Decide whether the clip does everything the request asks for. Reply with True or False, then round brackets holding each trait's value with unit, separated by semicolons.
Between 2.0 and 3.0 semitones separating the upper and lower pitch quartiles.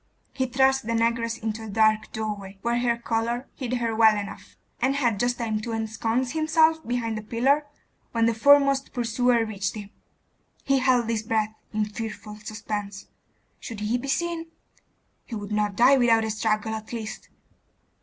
True (2.4 semitones)